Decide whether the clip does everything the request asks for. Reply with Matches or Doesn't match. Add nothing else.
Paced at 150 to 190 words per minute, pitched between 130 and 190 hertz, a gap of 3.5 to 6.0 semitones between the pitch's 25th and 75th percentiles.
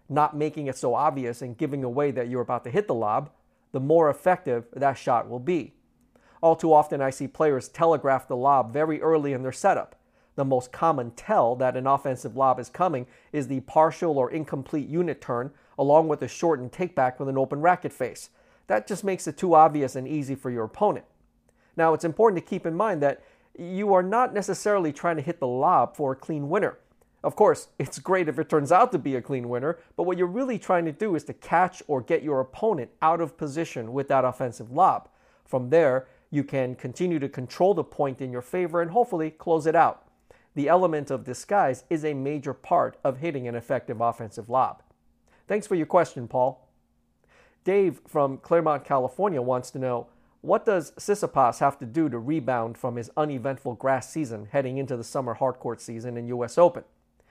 Doesn't match